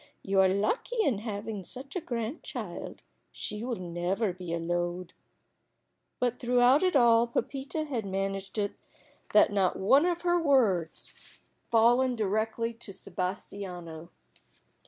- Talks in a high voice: Yes, high, 215 Hz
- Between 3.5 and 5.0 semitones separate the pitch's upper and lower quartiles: Yes, average, 4.7 semitones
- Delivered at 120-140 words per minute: Yes, slow, 135 wpm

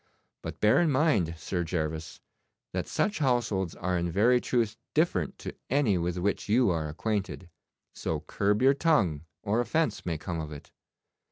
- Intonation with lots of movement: Yes, wide, 6.6 semitones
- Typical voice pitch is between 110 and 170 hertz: No, low, 100 Hz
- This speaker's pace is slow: No, average, 165 wpm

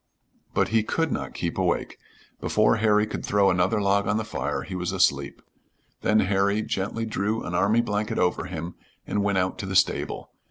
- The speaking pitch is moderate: No, low, 100 Hz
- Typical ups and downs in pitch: No, narrow, 2.3 semitones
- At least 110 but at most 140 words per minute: No, average, 190 wpm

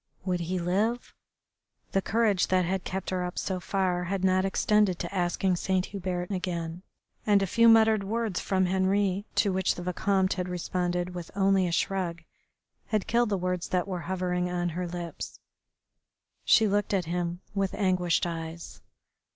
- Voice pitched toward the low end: No, medium, 185 Hz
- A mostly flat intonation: Yes, narrow, 1.8 semitones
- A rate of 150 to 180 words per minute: Yes, average, 165 wpm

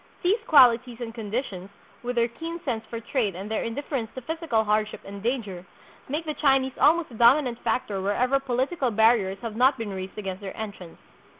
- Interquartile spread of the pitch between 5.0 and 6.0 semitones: No, average, 4.0 semitones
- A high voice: Yes, high, 235 Hz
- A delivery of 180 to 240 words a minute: Yes, average, 185 wpm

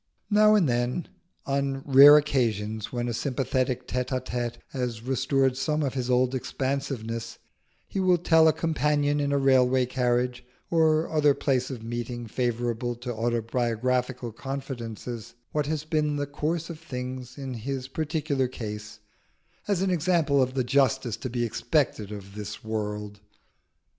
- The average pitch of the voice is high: No, low, 130 Hz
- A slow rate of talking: No, average, 150 wpm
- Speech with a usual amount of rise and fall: Yes, average, 3.2 semitones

